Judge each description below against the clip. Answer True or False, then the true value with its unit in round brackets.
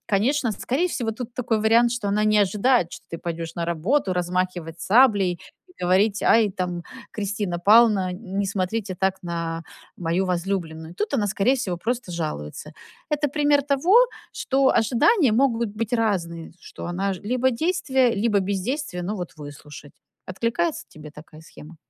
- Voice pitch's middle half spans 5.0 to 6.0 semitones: True (5.3 semitones)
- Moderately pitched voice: False (200 Hz)